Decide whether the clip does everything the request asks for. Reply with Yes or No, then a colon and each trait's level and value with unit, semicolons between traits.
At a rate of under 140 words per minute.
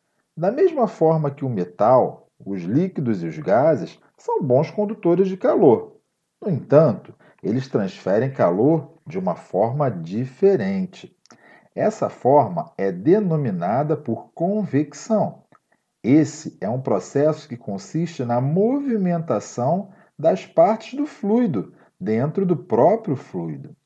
Yes: slow, 120 wpm